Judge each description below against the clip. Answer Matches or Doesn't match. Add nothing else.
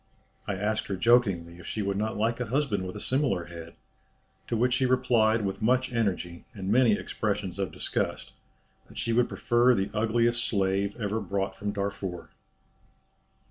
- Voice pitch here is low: Matches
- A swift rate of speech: Doesn't match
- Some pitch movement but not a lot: Matches